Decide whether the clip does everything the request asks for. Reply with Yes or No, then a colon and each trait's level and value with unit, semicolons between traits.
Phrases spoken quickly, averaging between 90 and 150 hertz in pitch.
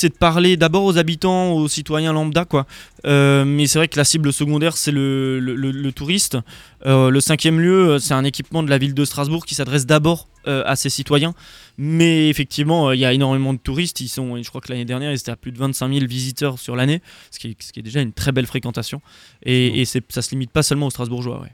Yes: fast, 250 wpm; medium, 140 Hz